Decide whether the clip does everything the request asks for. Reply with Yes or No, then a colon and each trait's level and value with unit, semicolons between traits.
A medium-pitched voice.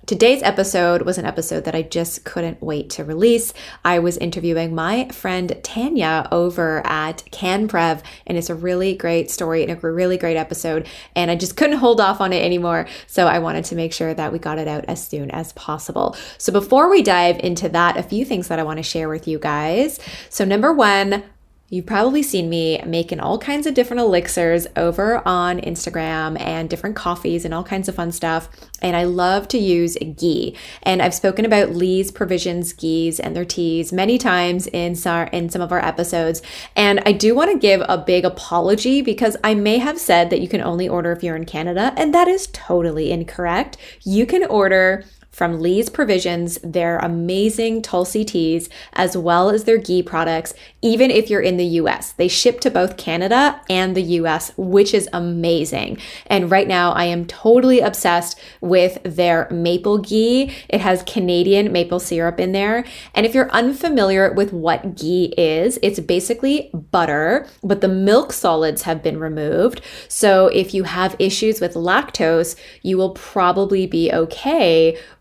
Yes: medium, 180 Hz